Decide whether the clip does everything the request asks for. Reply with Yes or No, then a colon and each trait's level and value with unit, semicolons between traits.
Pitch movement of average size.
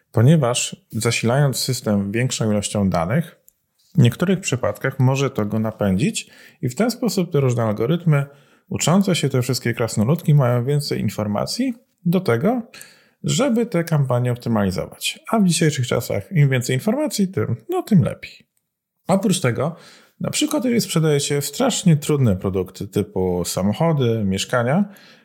No: wide, 8.1 semitones